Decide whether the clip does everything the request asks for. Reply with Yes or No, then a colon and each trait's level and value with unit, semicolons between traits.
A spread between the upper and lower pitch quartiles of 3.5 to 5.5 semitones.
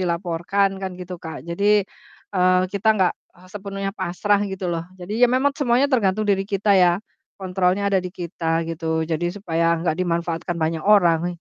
No: average, 2.9 semitones